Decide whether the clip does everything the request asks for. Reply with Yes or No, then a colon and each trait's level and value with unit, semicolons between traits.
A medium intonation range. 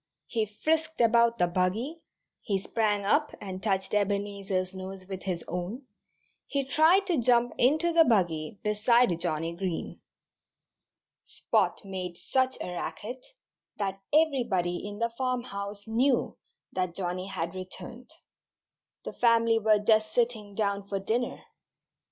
Yes: average, 4.4 semitones